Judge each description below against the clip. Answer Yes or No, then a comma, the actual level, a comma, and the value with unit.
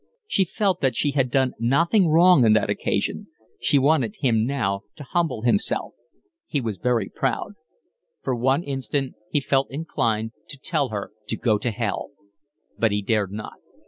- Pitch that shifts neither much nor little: Yes, average, 4.6 semitones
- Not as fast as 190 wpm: Yes, average, 170 wpm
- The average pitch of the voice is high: No, low, 130 Hz